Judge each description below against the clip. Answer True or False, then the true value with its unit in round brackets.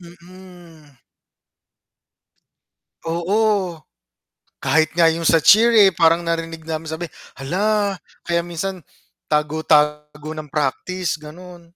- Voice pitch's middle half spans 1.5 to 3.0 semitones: True (2.7 semitones)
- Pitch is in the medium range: True (170 Hz)